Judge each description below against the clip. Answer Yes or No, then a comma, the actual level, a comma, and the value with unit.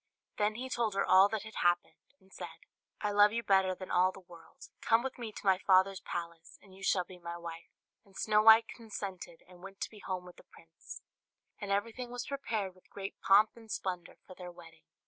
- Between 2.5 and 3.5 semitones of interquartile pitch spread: Yes, average, 3.1 semitones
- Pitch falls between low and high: No, high, 195 Hz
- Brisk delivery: Yes, fast, 210 wpm